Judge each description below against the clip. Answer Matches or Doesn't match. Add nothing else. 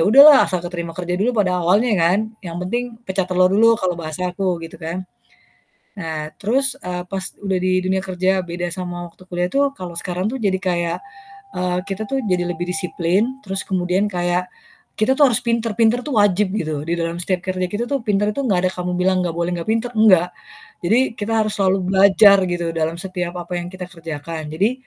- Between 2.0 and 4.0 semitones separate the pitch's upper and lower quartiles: Matches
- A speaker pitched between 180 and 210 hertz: Matches